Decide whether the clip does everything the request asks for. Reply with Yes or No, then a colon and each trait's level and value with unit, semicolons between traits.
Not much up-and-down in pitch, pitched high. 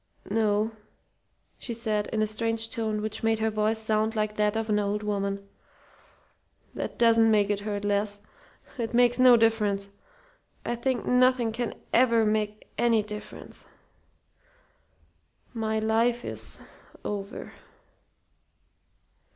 Yes: narrow, 1.5 semitones; high, 220 Hz